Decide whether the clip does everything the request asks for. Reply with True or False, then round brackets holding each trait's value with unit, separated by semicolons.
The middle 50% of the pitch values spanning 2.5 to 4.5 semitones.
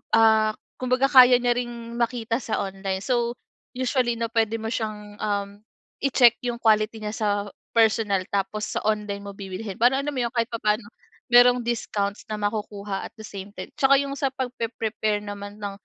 True (2.8 semitones)